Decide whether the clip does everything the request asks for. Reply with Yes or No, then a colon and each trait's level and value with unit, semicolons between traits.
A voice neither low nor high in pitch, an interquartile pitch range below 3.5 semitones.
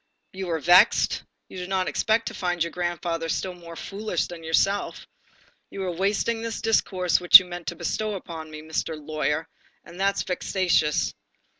Yes: medium, 180 Hz; average, 2.7 semitones